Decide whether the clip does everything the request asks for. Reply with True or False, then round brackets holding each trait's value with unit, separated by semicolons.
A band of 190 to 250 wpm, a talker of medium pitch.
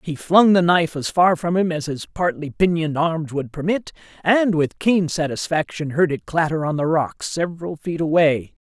True (195 wpm; 160 Hz)